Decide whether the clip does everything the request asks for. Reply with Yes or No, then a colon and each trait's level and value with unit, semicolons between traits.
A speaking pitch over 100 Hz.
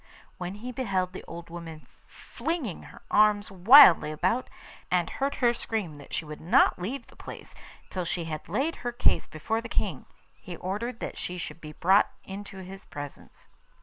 Yes: high, 190 Hz